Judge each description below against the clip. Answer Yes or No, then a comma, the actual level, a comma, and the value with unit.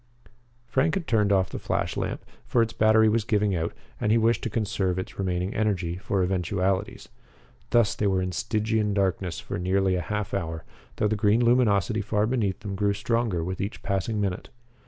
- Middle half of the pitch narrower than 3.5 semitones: Yes, average, 2.9 semitones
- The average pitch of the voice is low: Yes, low, 100 Hz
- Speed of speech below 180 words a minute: No, average, 185 wpm